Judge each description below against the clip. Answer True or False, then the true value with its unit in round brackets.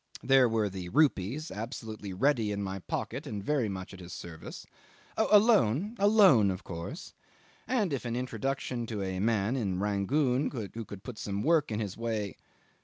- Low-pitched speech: True (110 Hz)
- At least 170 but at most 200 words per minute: True (180 wpm)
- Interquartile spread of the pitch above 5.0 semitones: True (5.6 semitones)